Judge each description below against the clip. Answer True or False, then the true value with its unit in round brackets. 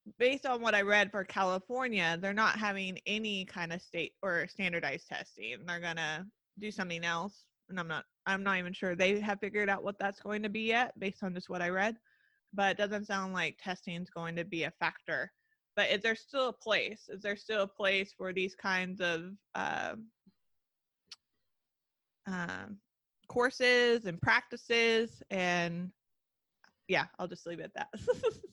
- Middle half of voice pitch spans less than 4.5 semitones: True (3.5 semitones)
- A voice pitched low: False (195 Hz)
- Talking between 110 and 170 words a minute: False (180 wpm)